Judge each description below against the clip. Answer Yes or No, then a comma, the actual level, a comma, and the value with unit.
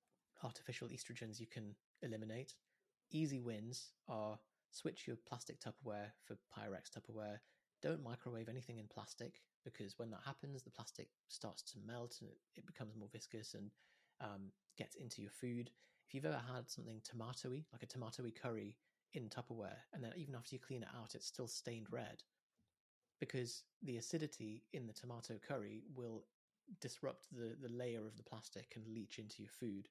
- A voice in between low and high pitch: No, low, 115 Hz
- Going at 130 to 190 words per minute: Yes, average, 170 wpm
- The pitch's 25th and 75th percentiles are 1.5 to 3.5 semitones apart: Yes, average, 2.7 semitones